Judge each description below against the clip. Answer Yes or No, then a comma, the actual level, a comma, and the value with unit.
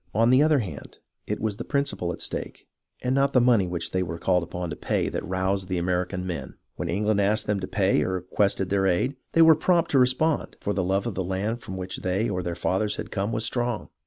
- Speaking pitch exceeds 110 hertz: No, low, 100 Hz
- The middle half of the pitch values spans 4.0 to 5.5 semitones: Yes, average, 4.7 semitones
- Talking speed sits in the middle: No, fast, 245 wpm